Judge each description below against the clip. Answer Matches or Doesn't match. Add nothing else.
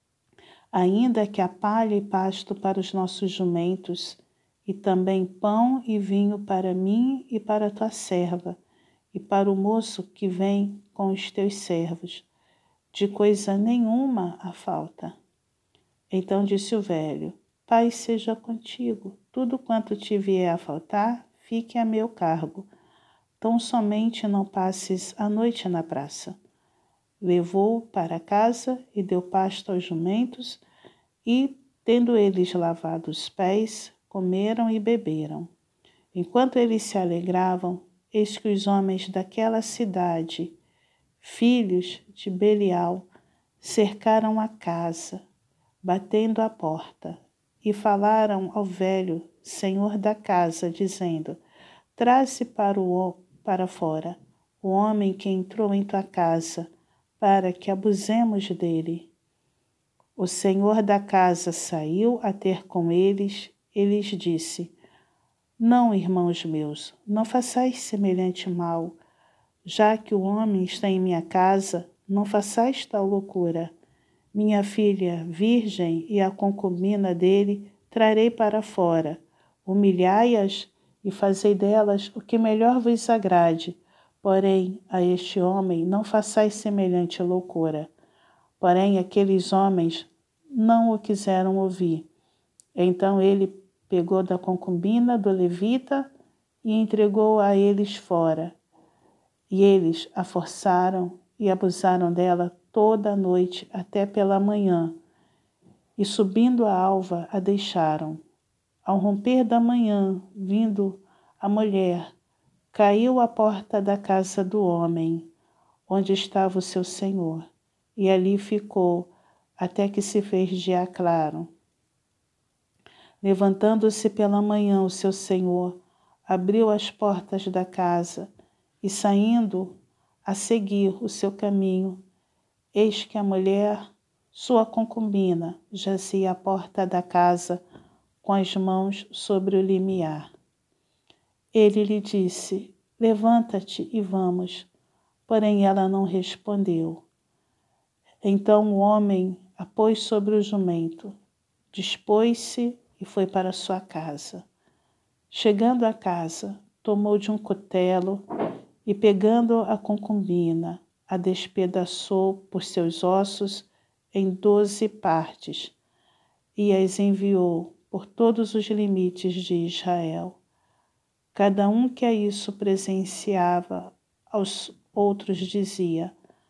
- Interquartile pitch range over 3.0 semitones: Doesn't match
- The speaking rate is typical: Doesn't match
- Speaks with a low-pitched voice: Doesn't match